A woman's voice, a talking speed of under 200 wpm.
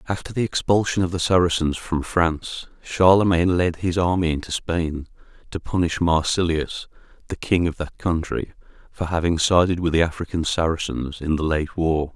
No: male; average, 165 wpm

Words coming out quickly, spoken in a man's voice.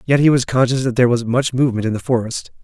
Yes: fast, 275 wpm; male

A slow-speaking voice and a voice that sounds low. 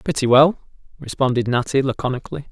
Yes: slow, 120 wpm; low, 130 Hz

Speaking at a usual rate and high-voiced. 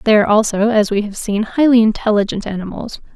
Yes: average, 190 wpm; high, 210 Hz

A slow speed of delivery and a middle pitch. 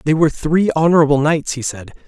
No: fast, 205 wpm; medium, 150 Hz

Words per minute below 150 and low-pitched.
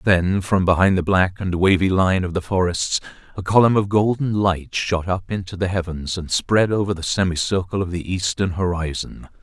No: average, 190 wpm; very low, 95 Hz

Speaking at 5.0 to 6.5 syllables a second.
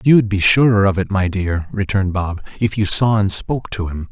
Yes: 5.5 syllables/s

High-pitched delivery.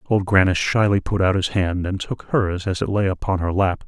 No: very low, 95 Hz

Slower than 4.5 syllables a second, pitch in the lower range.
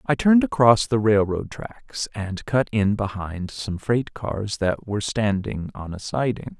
Yes: 4.1 syllables/s; low, 105 Hz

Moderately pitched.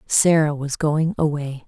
Yes: medium, 150 Hz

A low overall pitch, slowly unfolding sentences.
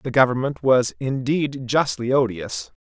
Yes: low, 125 Hz; slow, 125 wpm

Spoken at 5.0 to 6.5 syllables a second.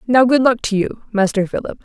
Yes: 5.5 syllables/s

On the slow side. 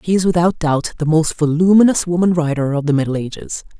No: fast, 205 wpm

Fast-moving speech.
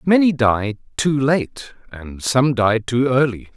No: average, 150 wpm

